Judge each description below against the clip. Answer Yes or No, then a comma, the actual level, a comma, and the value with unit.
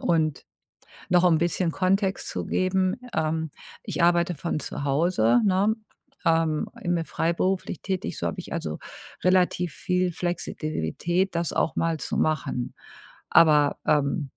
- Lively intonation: No, average, 2.8 semitones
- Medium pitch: Yes, medium, 170 Hz